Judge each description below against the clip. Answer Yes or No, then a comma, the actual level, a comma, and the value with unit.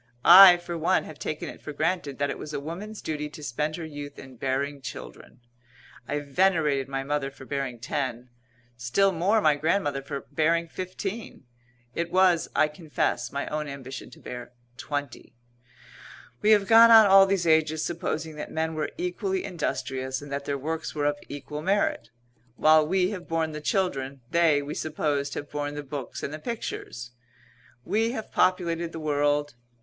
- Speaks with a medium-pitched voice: Yes, medium, 155 Hz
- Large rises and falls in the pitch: No, average, 3.6 semitones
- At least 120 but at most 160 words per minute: No, average, 175 wpm